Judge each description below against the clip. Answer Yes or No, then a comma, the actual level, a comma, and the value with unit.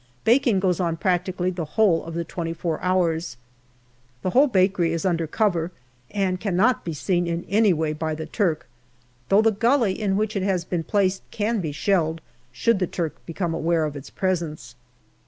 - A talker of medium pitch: Yes, medium, 180 Hz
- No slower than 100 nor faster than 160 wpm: No, average, 185 wpm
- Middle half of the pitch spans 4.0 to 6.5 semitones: No, average, 3.3 semitones